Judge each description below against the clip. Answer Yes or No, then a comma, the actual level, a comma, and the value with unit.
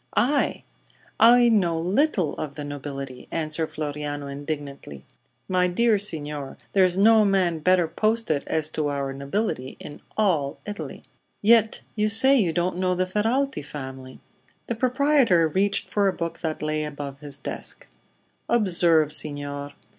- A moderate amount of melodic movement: No, wide, 6.3 semitones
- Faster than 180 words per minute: No, average, 145 wpm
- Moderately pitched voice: Yes, medium, 170 Hz